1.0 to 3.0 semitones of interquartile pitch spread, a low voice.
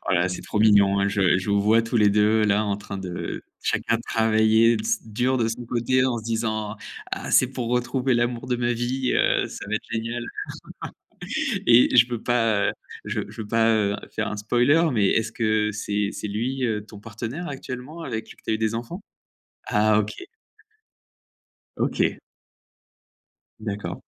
Yes: narrow, 2.5 semitones; low, 110 Hz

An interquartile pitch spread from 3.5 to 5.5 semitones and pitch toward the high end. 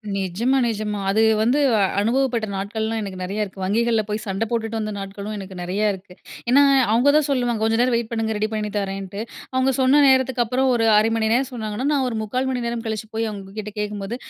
No: average, 3.1 semitones; high, 220 Hz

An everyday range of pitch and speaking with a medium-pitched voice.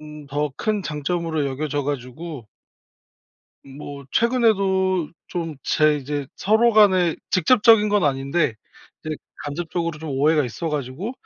Yes: average, 4.6 semitones; medium, 155 Hz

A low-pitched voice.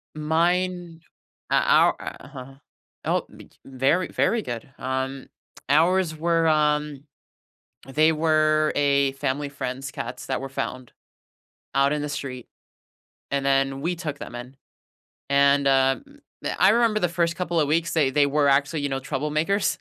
No: medium, 145 Hz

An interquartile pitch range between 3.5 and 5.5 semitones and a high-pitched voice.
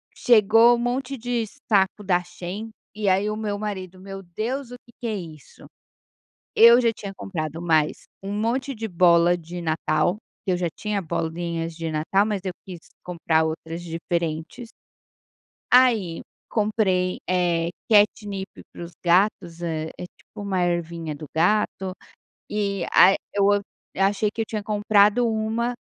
Yes: average, 4.0 semitones; high, 195 Hz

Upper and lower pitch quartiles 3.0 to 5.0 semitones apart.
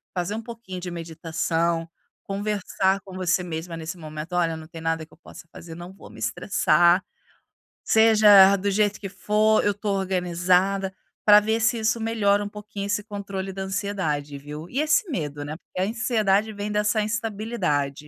Yes: average, 3.9 semitones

